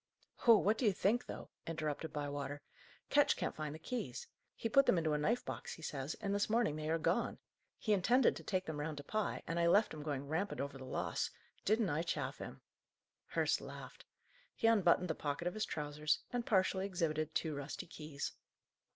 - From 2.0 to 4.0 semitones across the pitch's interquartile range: No, wide, 5.5 semitones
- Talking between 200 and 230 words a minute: Yes, fast, 205 wpm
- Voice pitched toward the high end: No, medium, 165 Hz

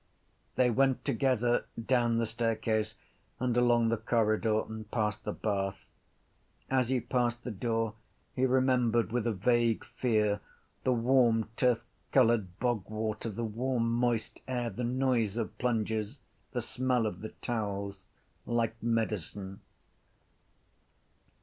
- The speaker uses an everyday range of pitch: No, narrow, 2.1 semitones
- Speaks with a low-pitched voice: Yes, low, 115 Hz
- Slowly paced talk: Yes, slow, 125 wpm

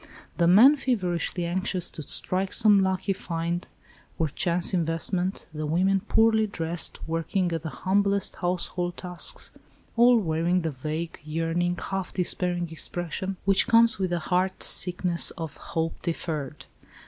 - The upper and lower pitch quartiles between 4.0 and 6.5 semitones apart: No, average, 2.7 semitones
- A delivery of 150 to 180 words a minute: No, slow, 135 wpm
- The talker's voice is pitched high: No, medium, 175 Hz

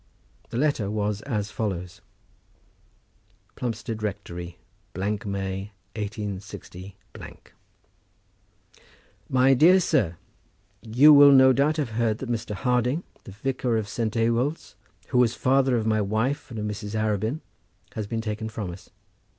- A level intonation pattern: No, average, 3.7 semitones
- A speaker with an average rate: No, slow, 130 wpm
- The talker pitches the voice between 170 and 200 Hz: No, low, 110 Hz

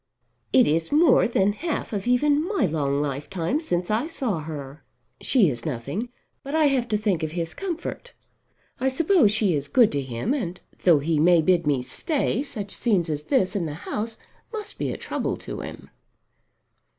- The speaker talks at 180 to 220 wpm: Yes, average, 185 wpm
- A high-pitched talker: Yes, high, 195 Hz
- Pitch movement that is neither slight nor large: No, wide, 9.0 semitones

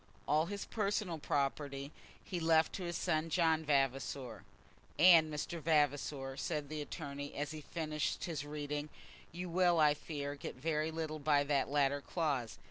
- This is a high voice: No, medium, 150 Hz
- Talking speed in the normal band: Yes, average, 155 wpm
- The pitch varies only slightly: Yes, narrow, 2.3 semitones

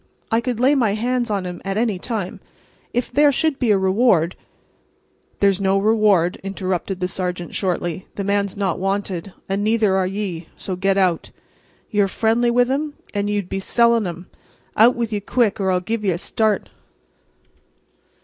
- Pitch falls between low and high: No, high, 200 Hz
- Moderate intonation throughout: Yes, average, 3.4 semitones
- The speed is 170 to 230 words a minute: Yes, average, 180 wpm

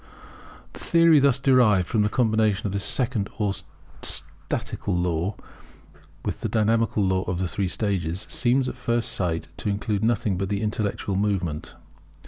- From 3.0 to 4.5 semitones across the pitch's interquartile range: Yes, average, 3.5 semitones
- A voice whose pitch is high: No, low, 105 Hz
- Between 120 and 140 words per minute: No, average, 155 wpm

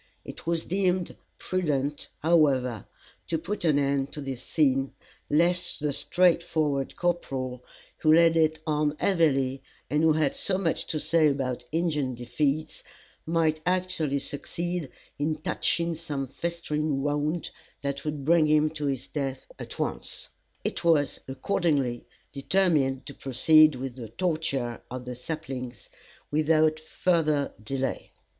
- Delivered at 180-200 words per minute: No, slow, 135 wpm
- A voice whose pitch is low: No, medium, 150 Hz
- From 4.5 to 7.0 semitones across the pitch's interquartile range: No, average, 3.3 semitones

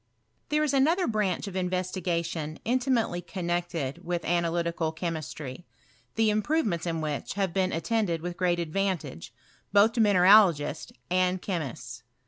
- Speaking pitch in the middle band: Yes, medium, 180 Hz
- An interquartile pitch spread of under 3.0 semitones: No, average, 3.6 semitones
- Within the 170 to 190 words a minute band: No, slow, 135 wpm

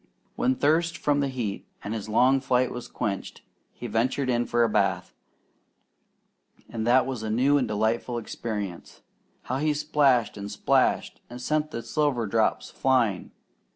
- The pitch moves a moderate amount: Yes, average, 3.7 semitones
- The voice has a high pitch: No, low, 120 Hz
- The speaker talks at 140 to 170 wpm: Yes, average, 155 wpm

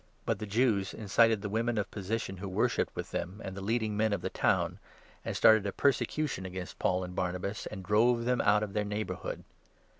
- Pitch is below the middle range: Yes, low, 105 Hz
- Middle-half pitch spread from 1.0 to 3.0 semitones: Yes, average, 2.7 semitones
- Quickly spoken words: Yes, fast, 215 wpm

